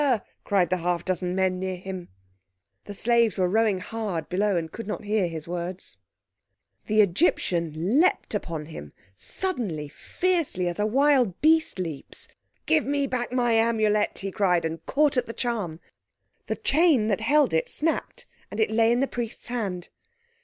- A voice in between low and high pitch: No, high, 210 Hz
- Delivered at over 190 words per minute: No, average, 165 wpm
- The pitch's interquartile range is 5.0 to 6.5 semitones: Yes, average, 5.3 semitones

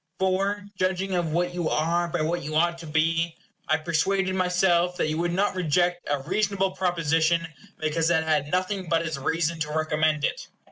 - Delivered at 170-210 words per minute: Yes, average, 185 wpm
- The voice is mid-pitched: Yes, medium, 170 Hz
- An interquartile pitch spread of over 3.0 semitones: No, narrow, 2.6 semitones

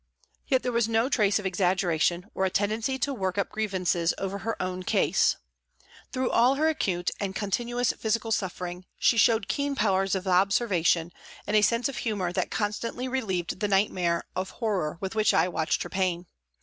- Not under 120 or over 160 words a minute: No, average, 180 wpm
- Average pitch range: Yes, average, 3.9 semitones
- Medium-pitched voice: No, high, 200 Hz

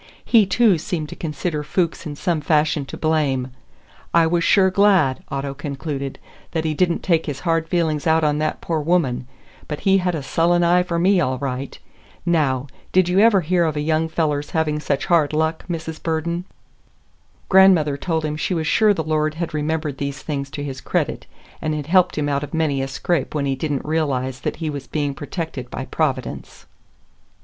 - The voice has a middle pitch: Yes, medium, 155 Hz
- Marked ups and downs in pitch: No, average, 3.0 semitones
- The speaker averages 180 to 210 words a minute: Yes, average, 200 wpm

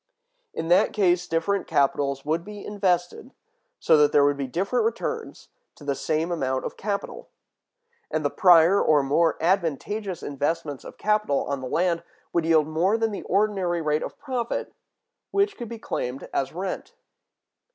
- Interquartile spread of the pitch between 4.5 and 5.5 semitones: Yes, average, 5.2 semitones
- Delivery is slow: No, average, 160 wpm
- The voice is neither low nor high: Yes, medium, 170 Hz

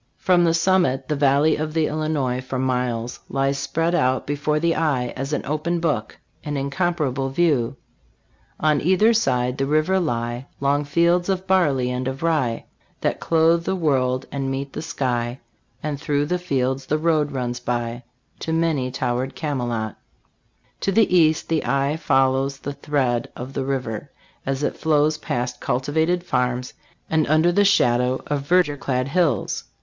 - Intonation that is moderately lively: Yes, average, 4.0 semitones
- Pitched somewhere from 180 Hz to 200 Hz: No, medium, 140 Hz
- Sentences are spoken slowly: No, average, 165 wpm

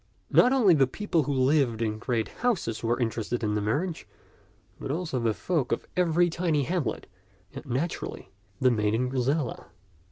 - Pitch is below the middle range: Yes, low, 130 Hz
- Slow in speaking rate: No, average, 160 wpm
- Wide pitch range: Yes, wide, 6.3 semitones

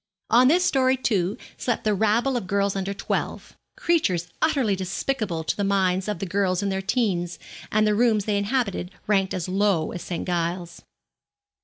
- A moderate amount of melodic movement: Yes, average, 3.7 semitones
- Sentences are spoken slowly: No, average, 170 wpm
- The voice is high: Yes, high, 200 Hz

